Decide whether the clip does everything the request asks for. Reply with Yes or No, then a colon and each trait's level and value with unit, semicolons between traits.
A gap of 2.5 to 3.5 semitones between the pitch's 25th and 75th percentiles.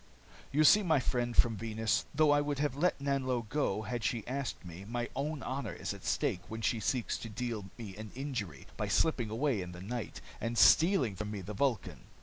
No: average, 4.6 semitones